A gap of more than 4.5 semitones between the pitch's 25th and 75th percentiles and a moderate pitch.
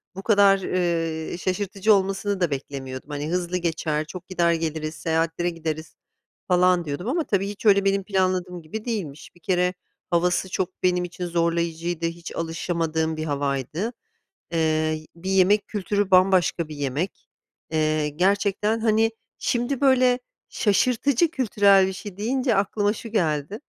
No: average, 3.8 semitones; medium, 180 Hz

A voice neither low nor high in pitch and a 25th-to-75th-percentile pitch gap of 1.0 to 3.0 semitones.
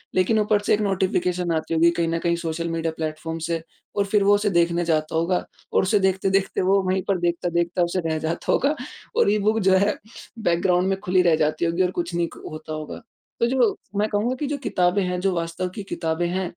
Yes: medium, 180 Hz; narrow, 2.6 semitones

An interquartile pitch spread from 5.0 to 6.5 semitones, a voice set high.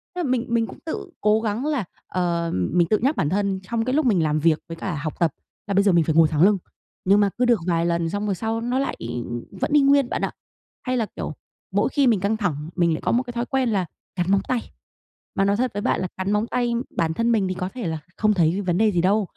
Yes: wide, 5.4 semitones; high, 200 Hz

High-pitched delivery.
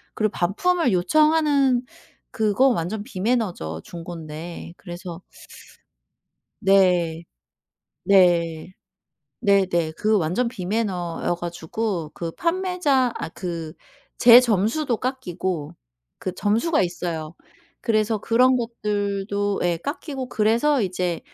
Yes: high, 200 Hz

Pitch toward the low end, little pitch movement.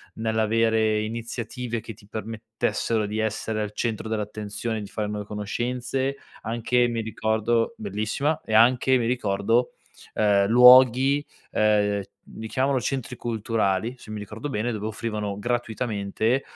Yes: low, 110 Hz; narrow, 2.1 semitones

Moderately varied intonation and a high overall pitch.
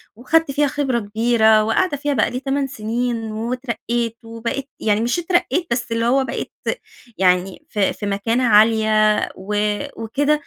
Yes: average, 3.8 semitones; high, 235 Hz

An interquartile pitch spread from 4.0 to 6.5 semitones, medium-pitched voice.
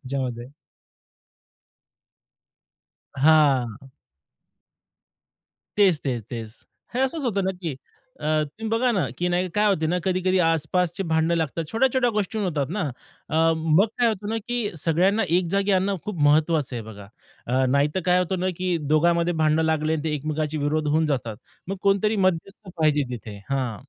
Yes: average, 4.7 semitones; medium, 160 Hz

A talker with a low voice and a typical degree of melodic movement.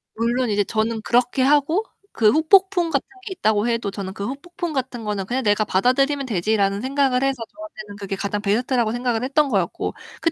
No: high, 240 Hz; average, 4.9 semitones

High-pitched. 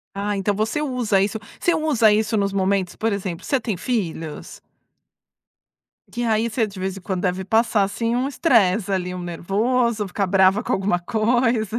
Yes: high, 210 Hz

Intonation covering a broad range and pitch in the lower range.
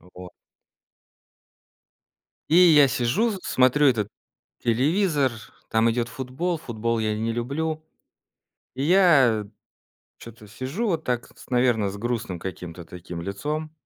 Yes: wide, 5.8 semitones; low, 125 Hz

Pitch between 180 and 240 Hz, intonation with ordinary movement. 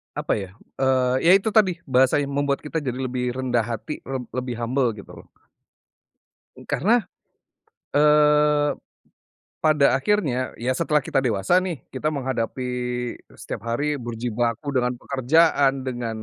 No: low, 130 Hz; average, 3.4 semitones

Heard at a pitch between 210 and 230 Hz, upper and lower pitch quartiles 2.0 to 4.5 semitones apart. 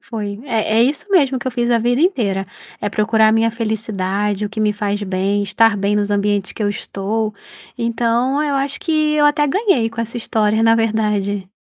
Yes: high, 220 Hz; average, 2.8 semitones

